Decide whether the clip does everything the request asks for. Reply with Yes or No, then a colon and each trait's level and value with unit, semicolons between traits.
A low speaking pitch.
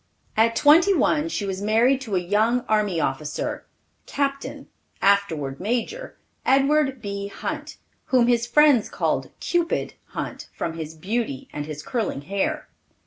No: high, 225 Hz